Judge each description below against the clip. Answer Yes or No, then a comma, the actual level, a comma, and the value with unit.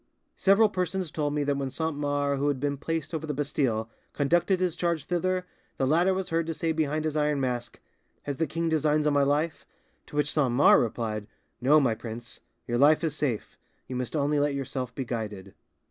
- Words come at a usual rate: No, fast, 210 wpm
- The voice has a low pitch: No, medium, 145 Hz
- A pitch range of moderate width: Yes, average, 3.4 semitones